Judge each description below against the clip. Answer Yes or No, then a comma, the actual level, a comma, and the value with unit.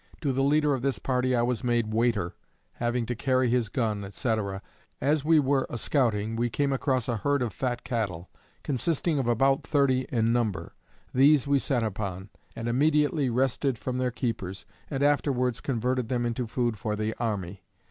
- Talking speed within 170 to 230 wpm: Yes, average, 180 wpm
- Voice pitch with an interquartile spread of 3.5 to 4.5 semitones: No, average, 3.1 semitones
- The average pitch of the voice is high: No, low, 125 Hz